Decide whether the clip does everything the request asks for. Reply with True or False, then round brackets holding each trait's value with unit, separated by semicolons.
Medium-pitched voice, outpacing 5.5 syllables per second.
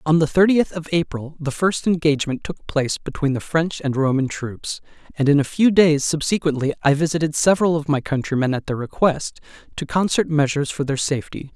True (150 Hz; 5.7 syllables/s)